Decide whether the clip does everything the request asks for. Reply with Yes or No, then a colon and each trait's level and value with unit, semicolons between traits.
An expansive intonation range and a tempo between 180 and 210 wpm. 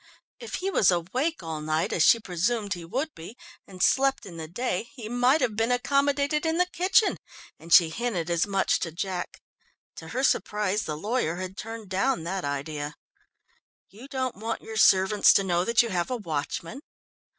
Yes: wide, 6.6 semitones; average, 185 wpm